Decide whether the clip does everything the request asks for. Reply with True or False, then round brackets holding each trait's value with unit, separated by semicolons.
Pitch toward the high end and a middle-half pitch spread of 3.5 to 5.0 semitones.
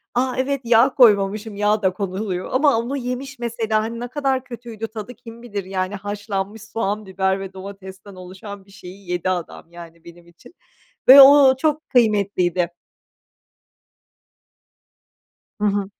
True (210 Hz; 4.1 semitones)